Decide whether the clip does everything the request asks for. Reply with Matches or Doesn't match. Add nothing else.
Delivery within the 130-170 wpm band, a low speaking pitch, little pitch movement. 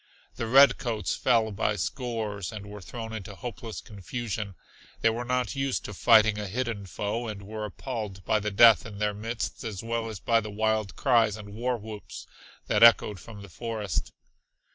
Doesn't match